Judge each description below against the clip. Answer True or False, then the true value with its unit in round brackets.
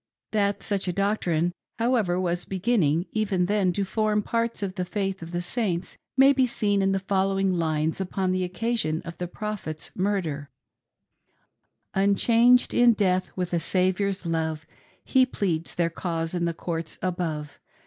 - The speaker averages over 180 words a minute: False (165 wpm)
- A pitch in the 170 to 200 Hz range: True (185 Hz)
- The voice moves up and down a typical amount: True (3.2 semitones)